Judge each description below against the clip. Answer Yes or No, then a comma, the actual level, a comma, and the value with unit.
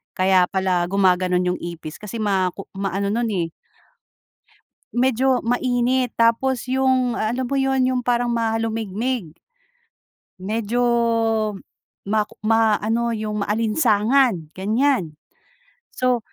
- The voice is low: No, high, 225 Hz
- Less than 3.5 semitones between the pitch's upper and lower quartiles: No, average, 4.2 semitones